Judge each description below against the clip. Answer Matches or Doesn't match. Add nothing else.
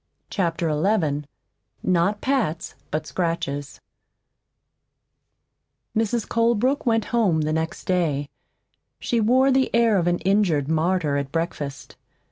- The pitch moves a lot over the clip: Matches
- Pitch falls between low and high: Matches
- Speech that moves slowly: Matches